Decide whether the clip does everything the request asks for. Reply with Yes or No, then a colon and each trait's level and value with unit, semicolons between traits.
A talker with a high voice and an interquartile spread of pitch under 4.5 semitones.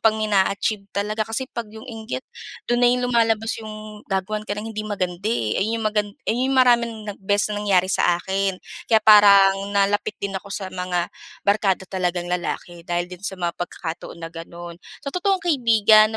Yes: high, 205 Hz; average, 2.9 semitones